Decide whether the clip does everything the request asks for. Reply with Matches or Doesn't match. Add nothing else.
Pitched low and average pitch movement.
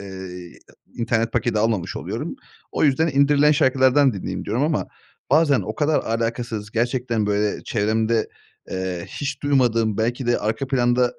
Matches